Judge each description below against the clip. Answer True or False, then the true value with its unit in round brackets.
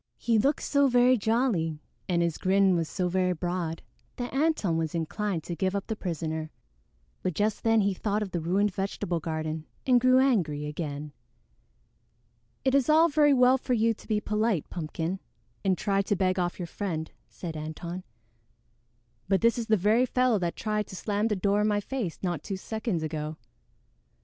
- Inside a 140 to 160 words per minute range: False (185 wpm)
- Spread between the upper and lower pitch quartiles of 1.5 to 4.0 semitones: False (5.0 semitones)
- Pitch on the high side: True (195 Hz)